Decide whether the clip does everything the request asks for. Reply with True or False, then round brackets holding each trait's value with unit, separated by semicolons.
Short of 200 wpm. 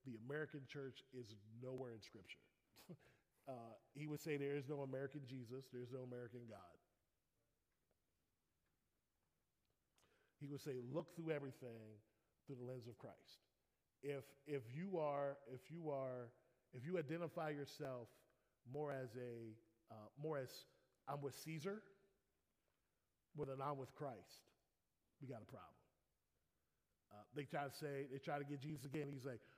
True (150 wpm)